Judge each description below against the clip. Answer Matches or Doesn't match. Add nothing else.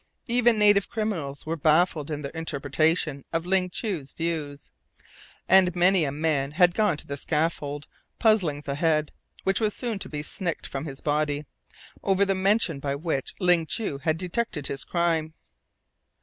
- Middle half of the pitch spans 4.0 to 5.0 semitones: Matches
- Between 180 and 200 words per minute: Doesn't match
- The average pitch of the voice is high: Doesn't match